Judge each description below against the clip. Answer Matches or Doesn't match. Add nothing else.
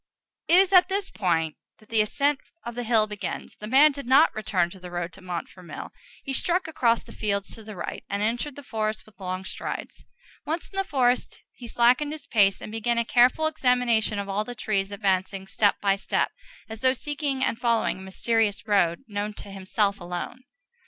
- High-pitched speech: Matches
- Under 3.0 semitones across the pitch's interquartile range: Doesn't match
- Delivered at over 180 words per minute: Matches